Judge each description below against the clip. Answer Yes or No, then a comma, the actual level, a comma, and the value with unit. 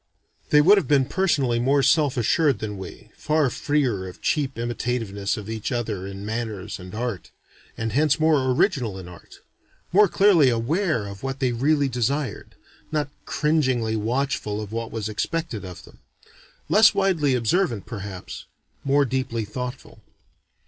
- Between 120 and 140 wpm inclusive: No, average, 150 wpm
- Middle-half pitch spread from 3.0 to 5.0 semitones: No, wide, 5.4 semitones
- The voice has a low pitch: Yes, low, 125 Hz